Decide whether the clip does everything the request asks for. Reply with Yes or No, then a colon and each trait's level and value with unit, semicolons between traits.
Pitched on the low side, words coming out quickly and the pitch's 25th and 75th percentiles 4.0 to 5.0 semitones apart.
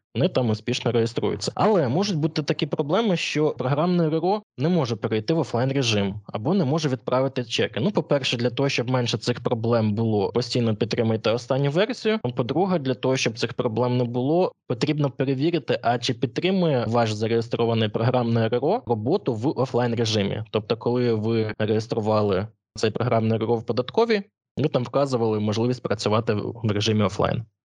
Yes: low, 125 Hz; fast, 160 wpm; average, 4.5 semitones